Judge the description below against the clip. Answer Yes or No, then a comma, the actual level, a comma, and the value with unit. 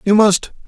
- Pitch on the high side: Yes, high, 205 Hz